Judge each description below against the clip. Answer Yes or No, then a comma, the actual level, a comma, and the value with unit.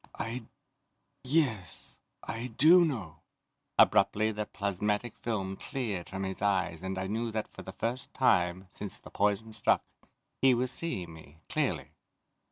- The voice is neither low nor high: No, low, 105 Hz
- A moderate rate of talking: Yes, average, 145 wpm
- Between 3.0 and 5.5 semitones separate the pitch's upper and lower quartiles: Yes, average, 4.1 semitones